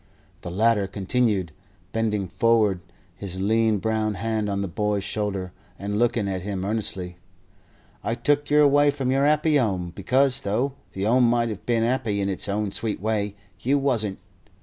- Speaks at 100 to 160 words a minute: No, average, 170 wpm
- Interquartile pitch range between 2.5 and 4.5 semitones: Yes, average, 3.3 semitones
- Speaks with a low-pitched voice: Yes, low, 110 Hz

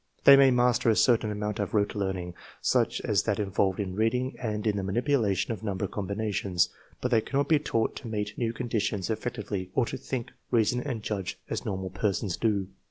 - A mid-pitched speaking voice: No, low, 105 Hz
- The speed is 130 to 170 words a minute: No, fast, 205 wpm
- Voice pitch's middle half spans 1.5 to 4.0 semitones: Yes, average, 3.5 semitones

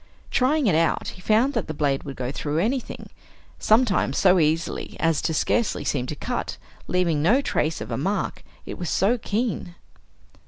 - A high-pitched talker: No, medium, 175 Hz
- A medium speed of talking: Yes, average, 180 wpm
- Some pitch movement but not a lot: No, wide, 6.4 semitones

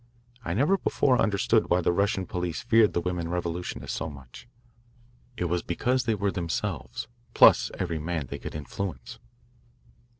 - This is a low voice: Yes, very low, 90 Hz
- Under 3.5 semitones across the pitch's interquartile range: No, average, 3.8 semitones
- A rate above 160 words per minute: No, average, 155 wpm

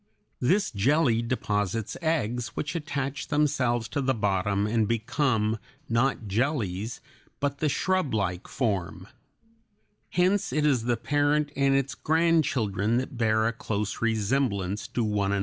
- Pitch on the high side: No, low, 120 Hz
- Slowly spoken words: No, average, 145 wpm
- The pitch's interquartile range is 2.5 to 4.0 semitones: No, average, 5.2 semitones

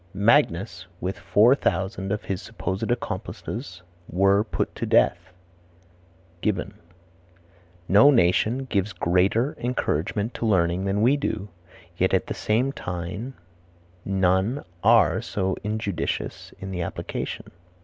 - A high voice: No, low, 100 Hz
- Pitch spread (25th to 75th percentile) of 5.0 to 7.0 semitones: No, average, 3.6 semitones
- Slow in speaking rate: Yes, slow, 120 wpm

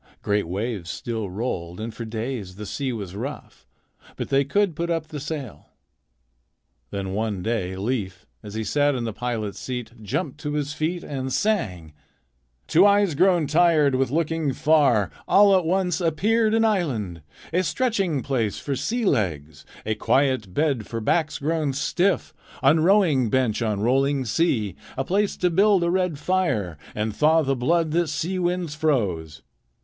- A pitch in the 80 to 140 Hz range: Yes, low, 135 Hz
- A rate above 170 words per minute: No, average, 165 wpm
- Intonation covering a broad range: Yes, wide, 7.5 semitones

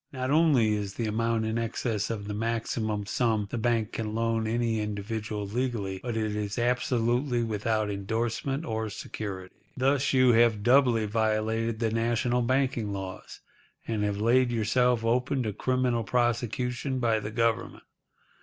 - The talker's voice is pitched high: No, low, 115 Hz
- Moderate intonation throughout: No, narrow, 2.2 semitones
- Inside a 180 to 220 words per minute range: No, average, 150 wpm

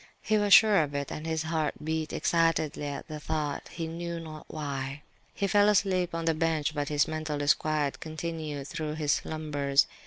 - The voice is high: No, medium, 155 Hz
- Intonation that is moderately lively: No, narrow, 1.9 semitones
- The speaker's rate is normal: Yes, average, 185 wpm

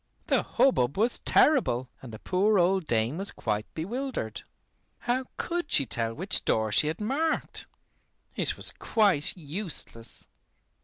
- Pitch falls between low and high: Yes, medium, 175 Hz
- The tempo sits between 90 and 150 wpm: Yes, average, 140 wpm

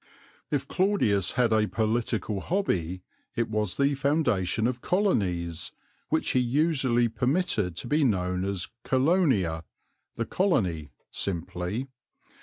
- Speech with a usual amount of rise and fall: No, wide, 7.2 semitones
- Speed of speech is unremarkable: No, slow, 115 wpm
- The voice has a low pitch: Yes, low, 115 Hz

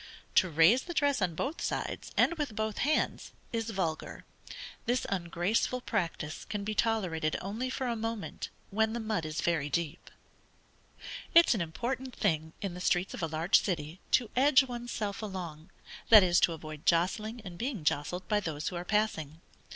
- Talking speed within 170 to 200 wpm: Yes, average, 180 wpm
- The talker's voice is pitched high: Yes, high, 195 Hz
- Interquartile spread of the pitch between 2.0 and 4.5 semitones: No, wide, 5.6 semitones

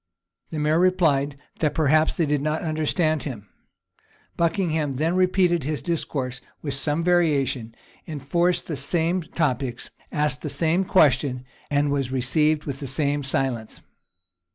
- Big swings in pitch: No, average, 3.2 semitones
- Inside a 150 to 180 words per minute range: No, slow, 135 wpm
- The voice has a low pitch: No, medium, 150 Hz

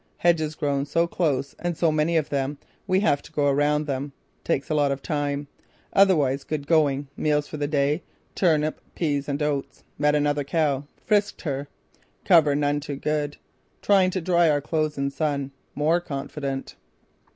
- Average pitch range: No, narrow, 2.0 semitones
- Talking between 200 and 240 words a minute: No, average, 170 wpm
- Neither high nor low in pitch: Yes, medium, 150 Hz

